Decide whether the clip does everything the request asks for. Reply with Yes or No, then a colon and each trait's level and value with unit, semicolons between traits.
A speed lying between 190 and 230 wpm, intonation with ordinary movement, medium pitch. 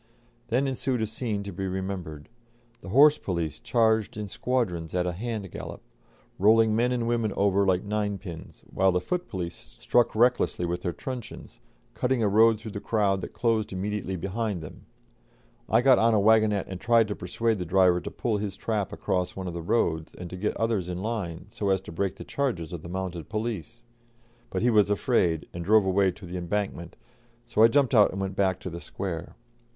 No: average, 200 wpm; average, 3.8 semitones; low, 100 Hz